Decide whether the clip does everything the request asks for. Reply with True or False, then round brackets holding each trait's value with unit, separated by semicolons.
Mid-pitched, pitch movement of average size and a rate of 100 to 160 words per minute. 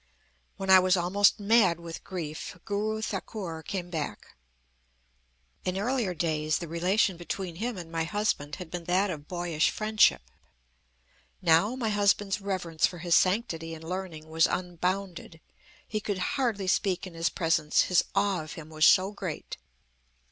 True (180 Hz; 3.5 semitones; 155 wpm)